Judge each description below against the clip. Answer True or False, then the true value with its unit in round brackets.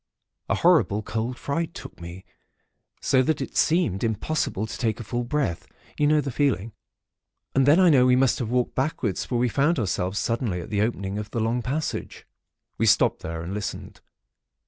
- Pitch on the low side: True (120 Hz)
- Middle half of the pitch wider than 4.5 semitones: True (5.2 semitones)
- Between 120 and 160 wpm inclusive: False (190 wpm)